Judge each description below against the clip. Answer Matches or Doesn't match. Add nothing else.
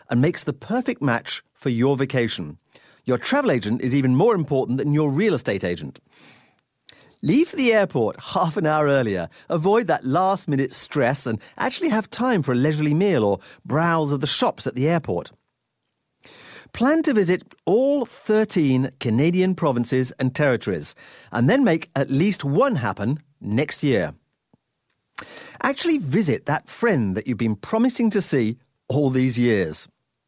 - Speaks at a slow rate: Doesn't match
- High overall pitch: Doesn't match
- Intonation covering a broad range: Matches